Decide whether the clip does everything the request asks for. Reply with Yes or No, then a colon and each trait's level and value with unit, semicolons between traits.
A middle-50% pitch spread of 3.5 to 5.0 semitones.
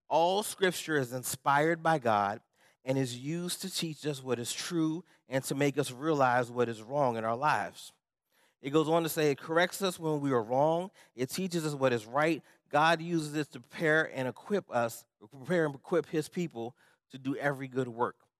Yes: average, 4.2 semitones